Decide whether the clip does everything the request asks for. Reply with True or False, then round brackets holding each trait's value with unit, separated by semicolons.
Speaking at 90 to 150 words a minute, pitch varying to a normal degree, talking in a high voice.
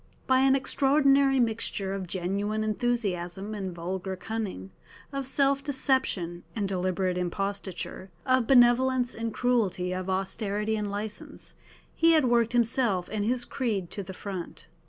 True (135 wpm; 4.8 semitones; 215 Hz)